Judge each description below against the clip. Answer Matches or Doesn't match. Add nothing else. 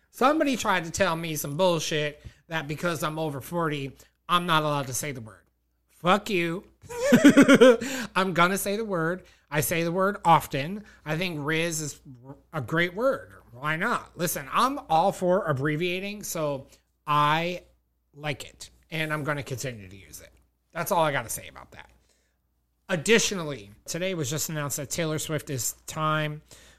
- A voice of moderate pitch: Matches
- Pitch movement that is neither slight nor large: Matches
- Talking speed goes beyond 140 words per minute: Matches